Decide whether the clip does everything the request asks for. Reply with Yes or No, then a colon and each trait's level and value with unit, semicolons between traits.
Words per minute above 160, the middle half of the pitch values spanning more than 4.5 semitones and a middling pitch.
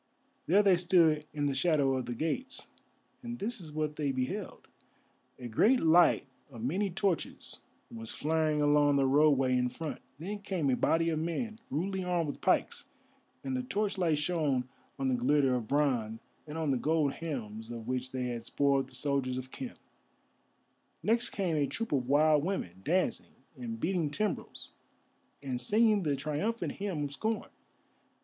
Yes: average, 170 wpm; wide, 5.5 semitones; medium, 150 Hz